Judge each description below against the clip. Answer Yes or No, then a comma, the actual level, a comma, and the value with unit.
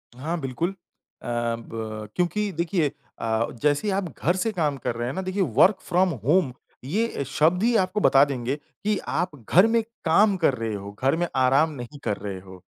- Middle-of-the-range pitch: Yes, medium, 150 Hz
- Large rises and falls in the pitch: Yes, wide, 7.5 semitones